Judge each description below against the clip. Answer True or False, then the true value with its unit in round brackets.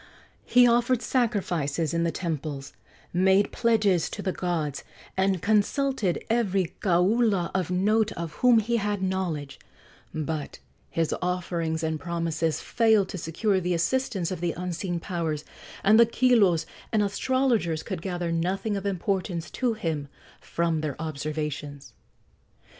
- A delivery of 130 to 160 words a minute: True (135 wpm)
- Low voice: False (180 Hz)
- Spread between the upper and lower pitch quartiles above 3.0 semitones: True (4.3 semitones)